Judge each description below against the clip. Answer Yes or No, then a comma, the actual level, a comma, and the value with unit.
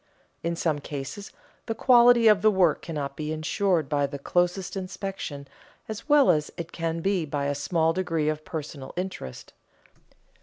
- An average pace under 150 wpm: No, average, 160 wpm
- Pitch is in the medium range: Yes, medium, 165 Hz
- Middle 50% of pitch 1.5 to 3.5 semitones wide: No, average, 4.4 semitones